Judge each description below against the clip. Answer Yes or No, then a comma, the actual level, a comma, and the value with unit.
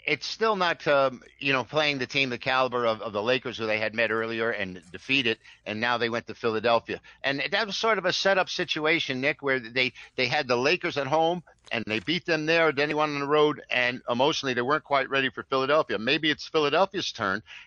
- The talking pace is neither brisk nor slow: No, fast, 235 wpm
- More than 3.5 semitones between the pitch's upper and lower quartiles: Yes, average, 4.4 semitones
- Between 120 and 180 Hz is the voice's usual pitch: Yes, low, 135 Hz